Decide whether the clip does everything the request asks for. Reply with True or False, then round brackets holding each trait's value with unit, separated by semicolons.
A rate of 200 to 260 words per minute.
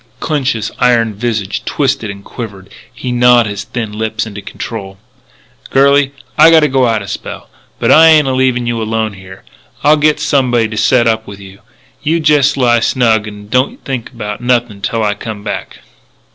False (180 wpm)